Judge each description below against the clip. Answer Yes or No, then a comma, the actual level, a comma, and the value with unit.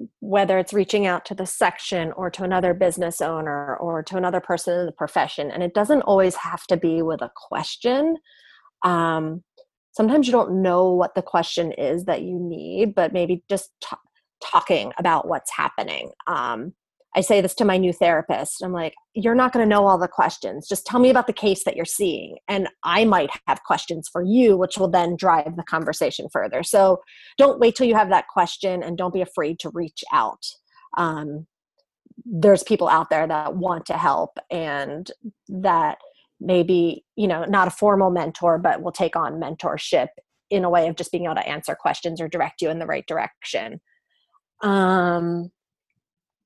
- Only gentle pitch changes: No, average, 3.7 semitones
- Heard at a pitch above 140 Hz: Yes, medium, 185 Hz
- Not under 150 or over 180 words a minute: No, average, 190 wpm